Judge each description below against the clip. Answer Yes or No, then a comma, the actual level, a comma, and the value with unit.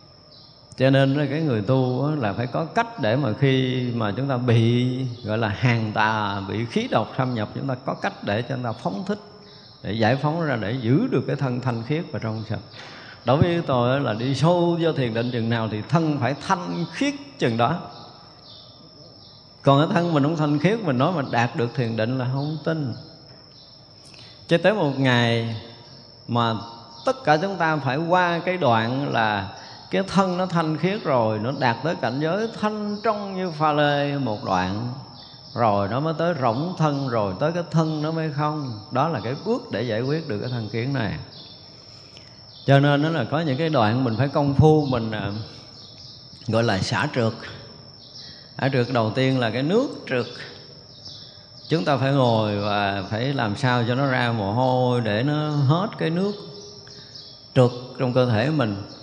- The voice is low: Yes, low, 130 Hz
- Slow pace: No, average, 195 wpm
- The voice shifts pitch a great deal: No, average, 4.4 semitones